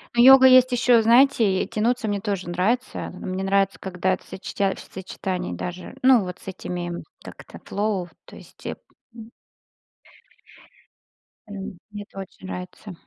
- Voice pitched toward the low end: No, high, 195 Hz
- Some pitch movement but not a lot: Yes, average, 3.8 semitones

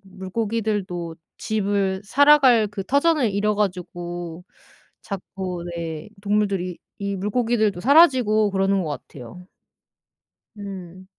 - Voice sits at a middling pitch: No, high, 200 Hz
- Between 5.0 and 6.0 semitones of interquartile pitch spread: No, average, 3.1 semitones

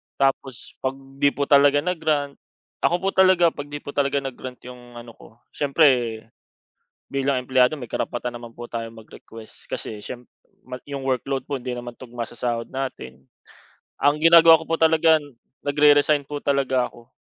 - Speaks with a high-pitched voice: No, low, 135 Hz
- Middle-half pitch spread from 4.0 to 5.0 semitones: No, average, 3.0 semitones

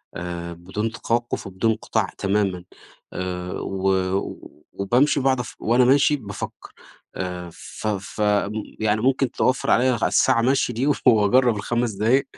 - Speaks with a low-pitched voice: Yes, low, 110 Hz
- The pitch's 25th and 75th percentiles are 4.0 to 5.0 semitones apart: Yes, average, 4.4 semitones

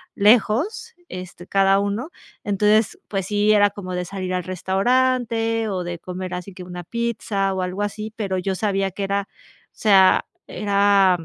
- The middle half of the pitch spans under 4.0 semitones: Yes, narrow, 2.4 semitones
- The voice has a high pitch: Yes, high, 200 Hz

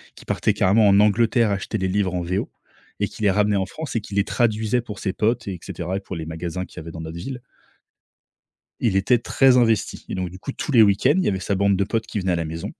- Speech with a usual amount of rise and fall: Yes, average, 3.3 semitones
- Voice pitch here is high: No, low, 100 Hz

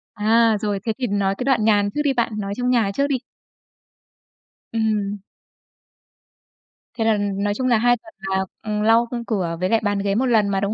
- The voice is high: Yes, high, 215 Hz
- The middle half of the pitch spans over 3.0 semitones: No, narrow, 2.6 semitones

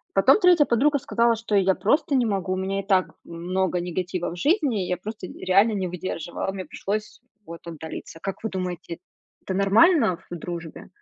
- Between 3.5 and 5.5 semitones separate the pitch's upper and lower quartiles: Yes, average, 3.8 semitones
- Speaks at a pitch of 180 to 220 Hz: Yes, high, 190 Hz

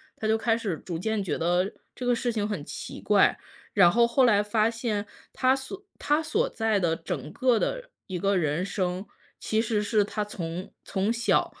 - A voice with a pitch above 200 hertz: Yes, high, 210 Hz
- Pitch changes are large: No, average, 4.3 semitones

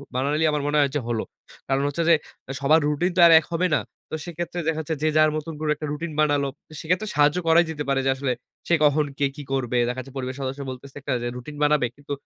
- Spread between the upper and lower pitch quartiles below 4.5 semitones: Yes, narrow, 2.6 semitones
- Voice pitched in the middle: Yes, medium, 150 Hz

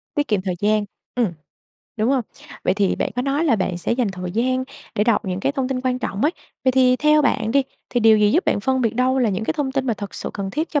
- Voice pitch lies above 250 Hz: No, high, 245 Hz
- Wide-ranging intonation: No, average, 4.2 semitones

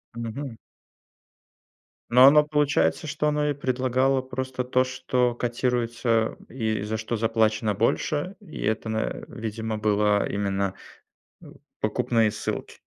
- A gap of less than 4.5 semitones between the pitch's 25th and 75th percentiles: Yes, average, 3.1 semitones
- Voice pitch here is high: No, low, 120 Hz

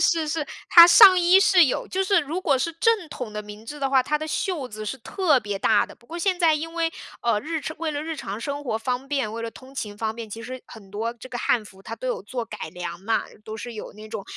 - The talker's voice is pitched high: Yes, very high, 255 Hz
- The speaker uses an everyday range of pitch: No, wide, 6.9 semitones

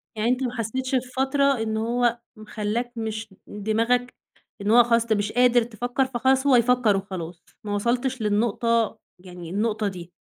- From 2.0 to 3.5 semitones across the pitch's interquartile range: Yes, average, 2.9 semitones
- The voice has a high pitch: Yes, high, 230 Hz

